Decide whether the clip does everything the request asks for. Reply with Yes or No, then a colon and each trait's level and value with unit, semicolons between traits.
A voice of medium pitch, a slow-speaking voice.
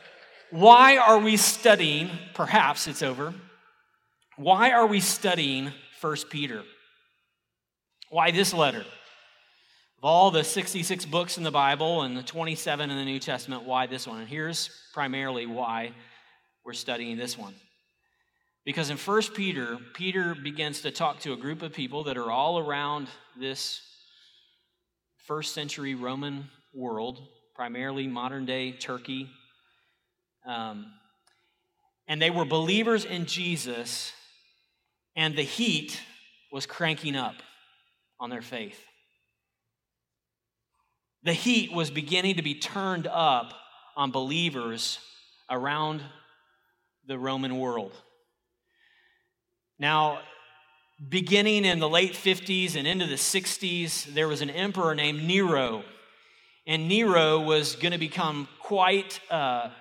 Yes: medium, 155 Hz; slow, 120 wpm